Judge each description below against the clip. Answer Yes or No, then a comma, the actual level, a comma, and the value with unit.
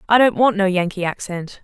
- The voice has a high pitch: Yes, high, 195 Hz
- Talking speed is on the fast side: Yes, fast, 220 wpm